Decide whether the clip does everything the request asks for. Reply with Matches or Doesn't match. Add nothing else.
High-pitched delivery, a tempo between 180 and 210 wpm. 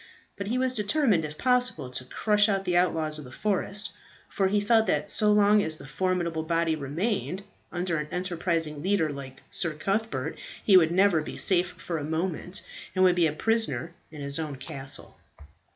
Doesn't match